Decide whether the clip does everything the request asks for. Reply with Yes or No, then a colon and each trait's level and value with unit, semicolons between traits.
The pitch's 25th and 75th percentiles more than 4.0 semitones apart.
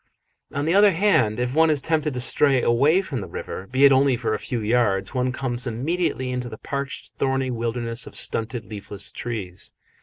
No: average, 3.4 semitones